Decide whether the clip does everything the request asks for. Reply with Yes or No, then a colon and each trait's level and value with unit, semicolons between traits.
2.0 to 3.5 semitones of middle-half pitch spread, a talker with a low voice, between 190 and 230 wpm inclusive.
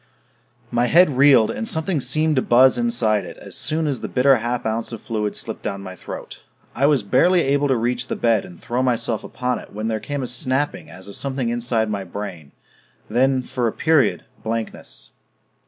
No: average, 4.0 semitones; low, 125 Hz; average, 200 wpm